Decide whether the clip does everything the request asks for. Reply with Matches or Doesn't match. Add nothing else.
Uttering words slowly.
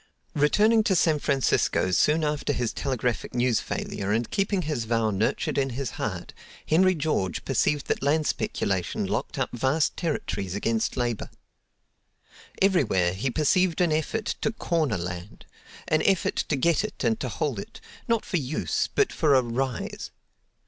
Doesn't match